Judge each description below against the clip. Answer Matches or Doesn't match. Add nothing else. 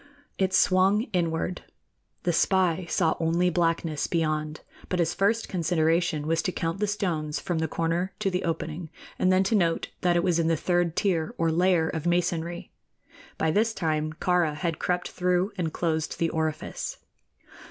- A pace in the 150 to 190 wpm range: Matches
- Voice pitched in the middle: Matches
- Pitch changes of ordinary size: Doesn't match